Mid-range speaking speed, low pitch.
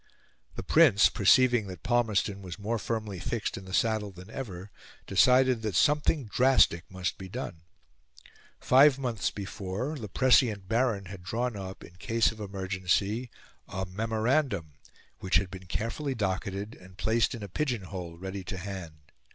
Yes: average, 155 wpm; low, 100 Hz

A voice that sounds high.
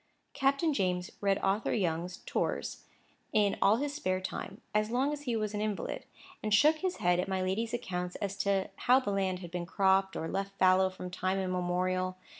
Yes: high, 195 Hz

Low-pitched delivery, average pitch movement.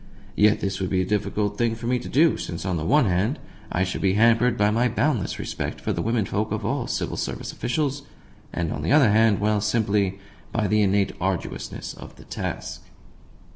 Yes: low, 105 Hz; average, 3.3 semitones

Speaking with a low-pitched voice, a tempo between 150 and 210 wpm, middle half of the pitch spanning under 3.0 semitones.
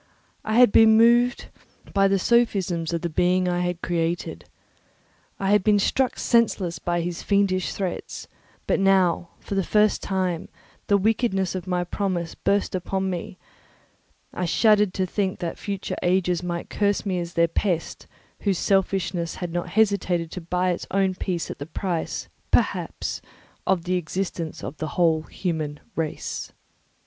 No: medium, 185 Hz; average, 160 wpm; narrow, 2.4 semitones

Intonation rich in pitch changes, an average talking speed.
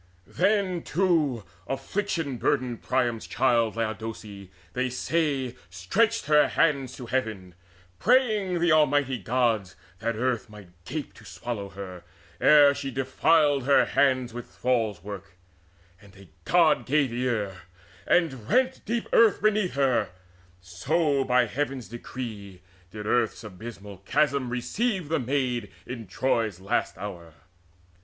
No: wide, 5.9 semitones; slow, 125 wpm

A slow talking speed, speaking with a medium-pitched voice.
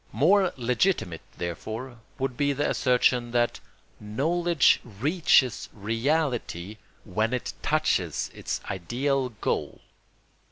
No: slow, 95 wpm; low, 125 Hz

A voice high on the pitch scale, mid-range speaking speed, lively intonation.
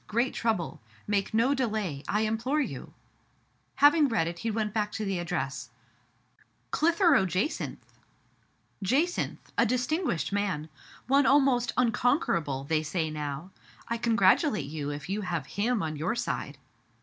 Yes: high, 210 Hz; average, 155 wpm; wide, 6.9 semitones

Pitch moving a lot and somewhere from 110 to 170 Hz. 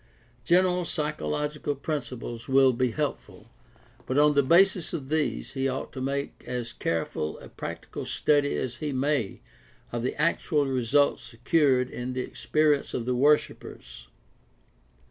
No: average, 3.1 semitones; medium, 140 Hz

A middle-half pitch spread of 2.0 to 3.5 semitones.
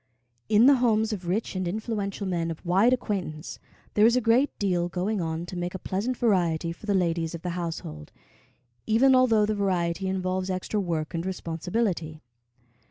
No: average, 4.1 semitones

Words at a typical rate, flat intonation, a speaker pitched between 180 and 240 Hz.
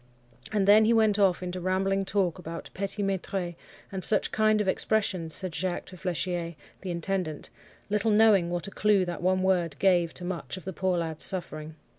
Yes: average, 190 wpm; narrow, 2.3 semitones; medium, 185 Hz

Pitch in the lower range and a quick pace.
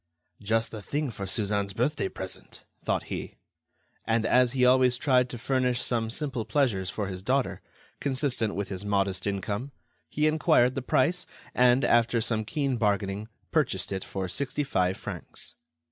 No: low, 120 Hz; average, 160 wpm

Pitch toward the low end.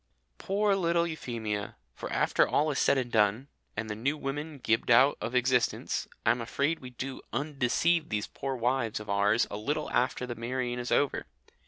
Yes: low, 125 Hz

